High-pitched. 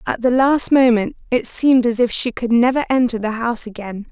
Yes: high, 240 Hz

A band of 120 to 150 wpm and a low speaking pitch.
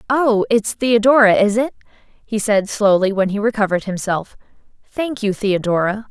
No: average, 145 wpm; high, 210 Hz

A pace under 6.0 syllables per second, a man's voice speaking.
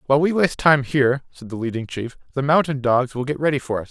No: 6.6 syllables/s; male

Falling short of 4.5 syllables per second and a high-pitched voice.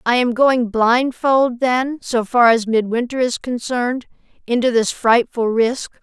Yes: 4.0 syllables/s; high, 240 Hz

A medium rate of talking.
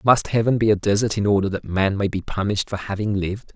No: fast, 255 wpm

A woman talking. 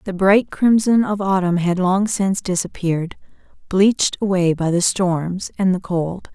Yes: female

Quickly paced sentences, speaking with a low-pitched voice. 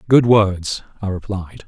No: average, 145 wpm; low, 100 Hz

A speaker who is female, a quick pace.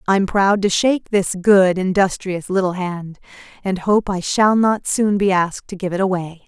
No: female; average, 195 wpm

